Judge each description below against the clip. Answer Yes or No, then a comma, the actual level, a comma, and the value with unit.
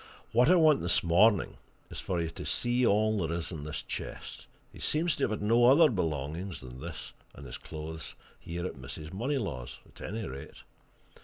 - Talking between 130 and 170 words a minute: No, average, 190 wpm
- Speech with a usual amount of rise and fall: No, wide, 7.2 semitones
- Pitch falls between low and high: No, very low, 90 Hz